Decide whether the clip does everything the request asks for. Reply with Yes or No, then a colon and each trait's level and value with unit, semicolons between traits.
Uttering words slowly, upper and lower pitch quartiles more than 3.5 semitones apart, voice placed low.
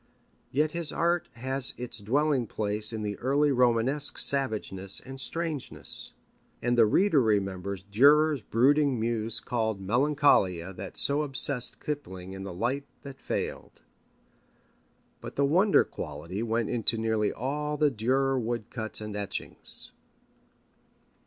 Yes: slow, 130 wpm; average, 5.1 semitones; low, 120 Hz